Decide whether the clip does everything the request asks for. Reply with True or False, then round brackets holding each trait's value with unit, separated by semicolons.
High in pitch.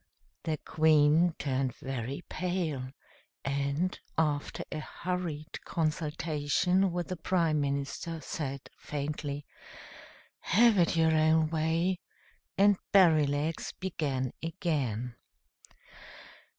False (155 Hz)